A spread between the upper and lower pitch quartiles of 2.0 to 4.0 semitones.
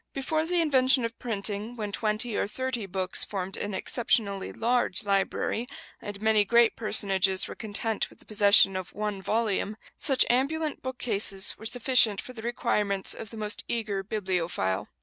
Yes: average, 3.3 semitones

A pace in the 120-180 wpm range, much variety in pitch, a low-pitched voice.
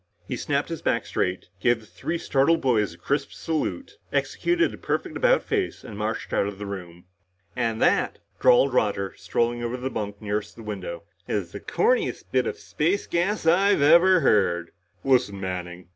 Yes: average, 175 wpm; wide, 8.8 semitones; low, 115 Hz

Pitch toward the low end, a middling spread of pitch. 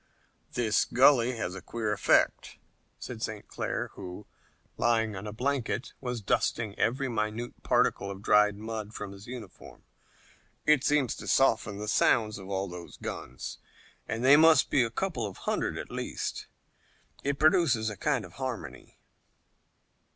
Yes: low, 115 Hz; average, 3.8 semitones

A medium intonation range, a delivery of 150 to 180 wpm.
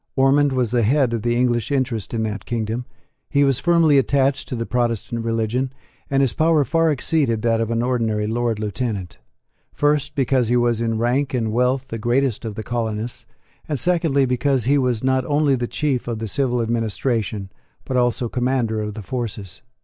No: average, 3.1 semitones; average, 190 wpm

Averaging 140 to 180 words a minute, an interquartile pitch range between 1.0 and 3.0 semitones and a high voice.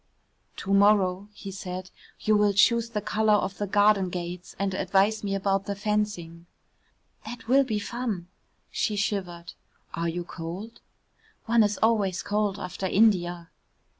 Yes: average, 145 wpm; narrow, 2.5 semitones; high, 200 Hz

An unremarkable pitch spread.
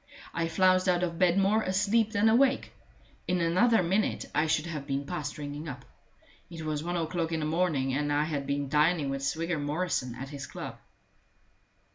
Yes: average, 3.9 semitones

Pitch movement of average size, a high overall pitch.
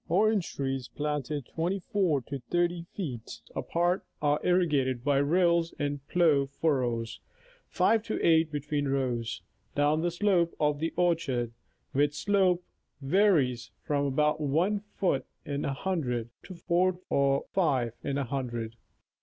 No: average, 4.3 semitones; medium, 150 Hz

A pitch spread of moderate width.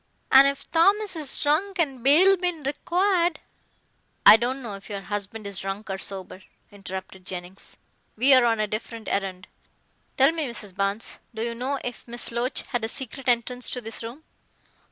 No: wide, 5.7 semitones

